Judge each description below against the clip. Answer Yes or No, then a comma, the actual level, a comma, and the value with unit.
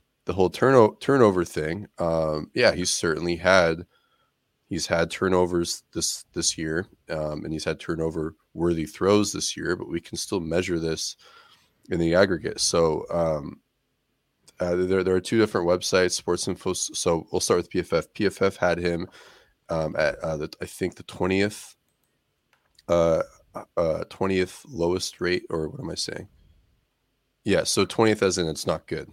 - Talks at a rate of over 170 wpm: No, average, 165 wpm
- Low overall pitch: Yes, very low, 85 Hz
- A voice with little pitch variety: Yes, narrow, 2.2 semitones